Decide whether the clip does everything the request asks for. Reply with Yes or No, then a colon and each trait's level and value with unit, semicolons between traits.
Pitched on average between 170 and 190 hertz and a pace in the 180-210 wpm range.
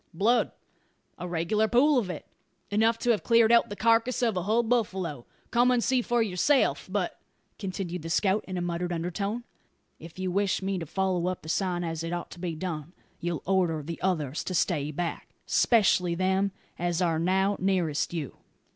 Yes: medium, 185 Hz; average, 190 wpm